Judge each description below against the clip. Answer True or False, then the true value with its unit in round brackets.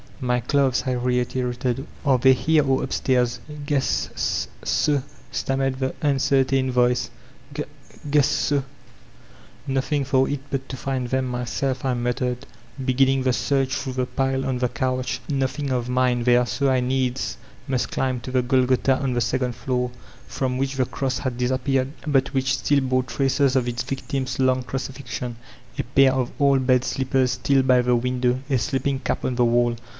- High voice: False (130 Hz)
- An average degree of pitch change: False (1.3 semitones)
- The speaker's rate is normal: True (170 wpm)